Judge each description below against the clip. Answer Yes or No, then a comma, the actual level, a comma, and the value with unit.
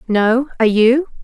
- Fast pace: No, average, 145 wpm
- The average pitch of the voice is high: Yes, high, 240 Hz